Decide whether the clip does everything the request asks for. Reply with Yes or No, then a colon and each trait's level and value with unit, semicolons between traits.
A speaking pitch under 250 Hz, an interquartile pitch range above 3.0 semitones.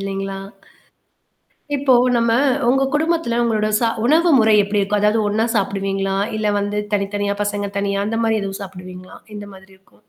No: high, 205 Hz; narrow, 2.5 semitones